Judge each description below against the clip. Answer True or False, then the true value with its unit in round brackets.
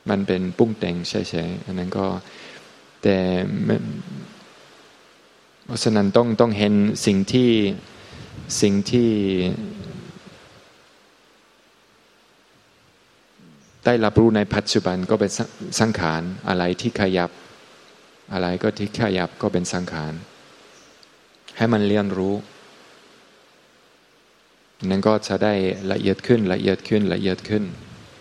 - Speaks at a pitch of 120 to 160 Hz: False (100 Hz)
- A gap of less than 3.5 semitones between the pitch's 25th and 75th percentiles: True (3.1 semitones)